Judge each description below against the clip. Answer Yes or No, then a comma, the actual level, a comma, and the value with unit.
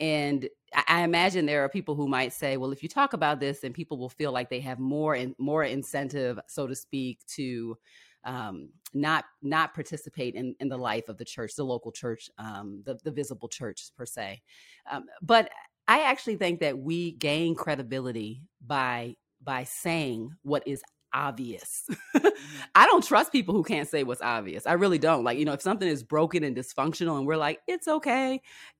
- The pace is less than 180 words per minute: No, average, 195 wpm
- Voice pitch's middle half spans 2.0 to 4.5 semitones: Yes, average, 4.0 semitones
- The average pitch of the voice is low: No, medium, 145 Hz